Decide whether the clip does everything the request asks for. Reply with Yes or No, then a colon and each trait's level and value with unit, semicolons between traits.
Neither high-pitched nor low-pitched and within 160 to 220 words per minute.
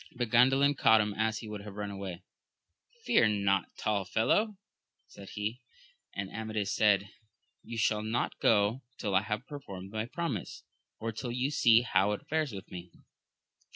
No: low, 110 Hz; average, 170 wpm